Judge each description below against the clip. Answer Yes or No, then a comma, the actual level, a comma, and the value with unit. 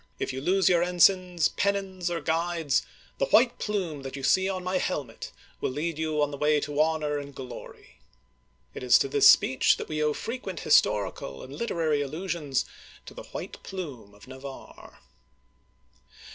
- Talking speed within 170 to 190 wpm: Yes, average, 180 wpm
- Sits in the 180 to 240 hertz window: No, medium, 155 Hz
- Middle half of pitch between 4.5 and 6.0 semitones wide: Yes, average, 4.9 semitones